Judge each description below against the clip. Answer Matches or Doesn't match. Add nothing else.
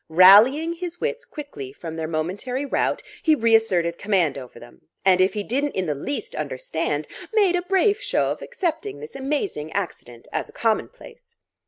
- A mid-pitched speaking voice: Doesn't match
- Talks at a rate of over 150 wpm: Matches